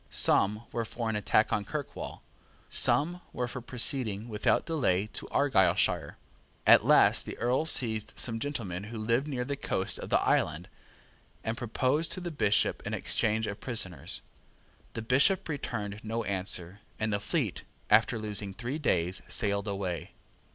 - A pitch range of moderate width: Yes, average, 4.0 semitones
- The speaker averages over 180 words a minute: No, average, 155 wpm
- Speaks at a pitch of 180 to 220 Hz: No, low, 110 Hz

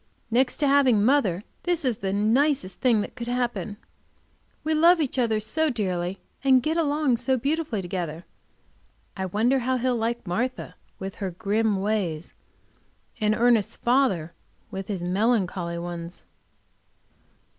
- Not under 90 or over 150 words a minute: Yes, average, 140 wpm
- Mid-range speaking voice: No, high, 225 Hz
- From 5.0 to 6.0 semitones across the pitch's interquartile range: Yes, wide, 5.4 semitones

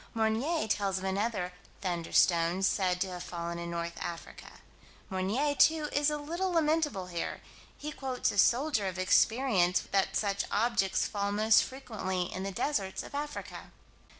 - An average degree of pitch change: No, wide, 6.6 semitones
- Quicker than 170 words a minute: No, average, 150 wpm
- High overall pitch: Yes, high, 200 Hz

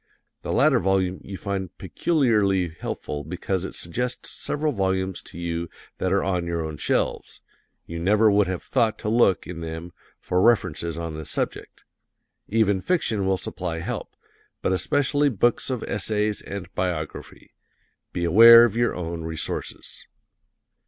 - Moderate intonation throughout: Yes, average, 4.3 semitones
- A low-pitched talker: Yes, very low, 95 Hz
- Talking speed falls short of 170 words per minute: Yes, average, 150 wpm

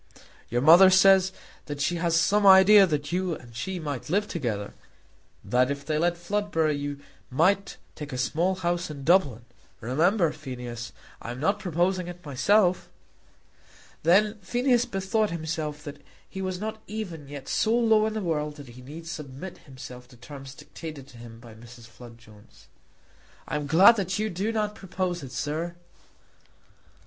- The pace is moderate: Yes, average, 165 wpm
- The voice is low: No, medium, 165 Hz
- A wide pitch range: Yes, wide, 5.8 semitones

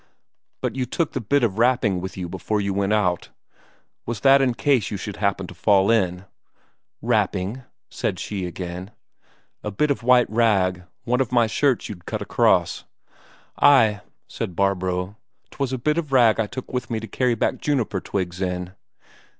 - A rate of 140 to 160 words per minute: No, average, 180 wpm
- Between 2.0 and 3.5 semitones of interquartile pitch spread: No, average, 4.9 semitones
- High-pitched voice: No, low, 105 Hz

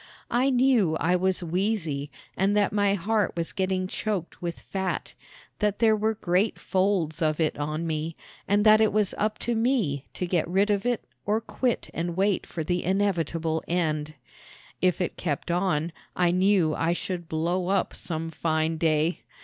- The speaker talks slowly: No, average, 175 wpm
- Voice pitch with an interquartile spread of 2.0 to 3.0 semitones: No, average, 4.0 semitones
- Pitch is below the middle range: No, medium, 180 Hz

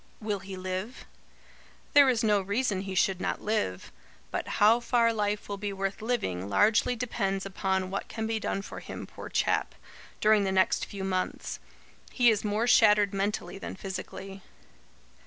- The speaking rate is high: No, average, 170 wpm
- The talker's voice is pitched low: No, high, 205 Hz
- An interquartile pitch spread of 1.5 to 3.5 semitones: Yes, narrow, 2.4 semitones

